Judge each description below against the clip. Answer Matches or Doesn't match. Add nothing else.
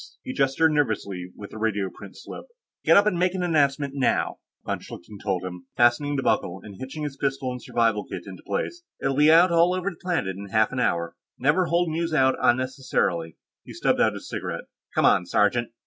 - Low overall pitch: Matches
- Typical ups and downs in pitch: Doesn't match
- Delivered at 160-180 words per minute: Doesn't match